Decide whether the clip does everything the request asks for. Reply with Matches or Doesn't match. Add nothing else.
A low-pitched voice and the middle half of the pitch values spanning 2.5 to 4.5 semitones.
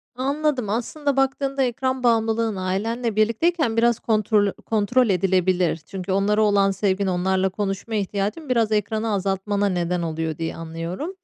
Doesn't match